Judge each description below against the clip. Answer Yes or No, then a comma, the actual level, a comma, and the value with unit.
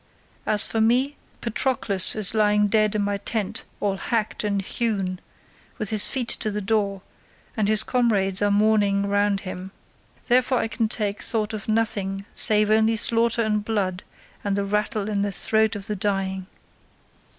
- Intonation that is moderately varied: No, narrow, 1.7 semitones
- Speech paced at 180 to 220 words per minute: No, average, 165 wpm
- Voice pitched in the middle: No, high, 210 Hz